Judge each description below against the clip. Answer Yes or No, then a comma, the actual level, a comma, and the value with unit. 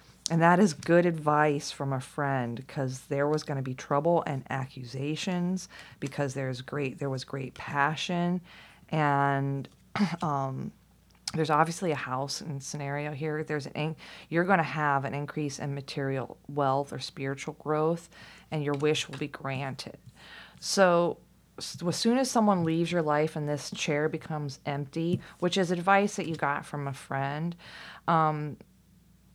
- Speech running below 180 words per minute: Yes, average, 160 wpm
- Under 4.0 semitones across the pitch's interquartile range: Yes, average, 3.1 semitones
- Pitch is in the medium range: Yes, medium, 150 Hz